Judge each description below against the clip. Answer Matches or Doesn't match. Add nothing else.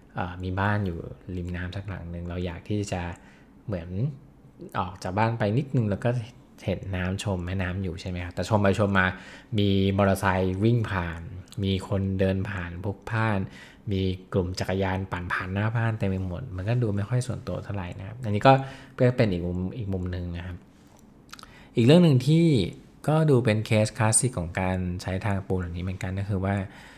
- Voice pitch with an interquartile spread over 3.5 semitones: Doesn't match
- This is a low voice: Matches